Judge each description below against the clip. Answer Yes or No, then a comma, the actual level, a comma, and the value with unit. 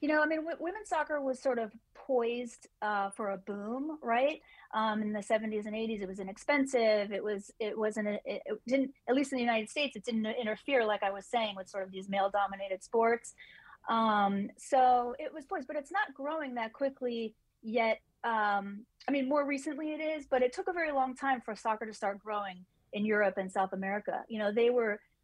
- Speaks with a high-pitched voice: Yes, high, 230 Hz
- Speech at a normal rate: No, fast, 215 wpm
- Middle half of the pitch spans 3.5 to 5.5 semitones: Yes, average, 4.6 semitones